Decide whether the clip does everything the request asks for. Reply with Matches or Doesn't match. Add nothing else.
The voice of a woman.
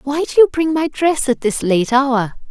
Matches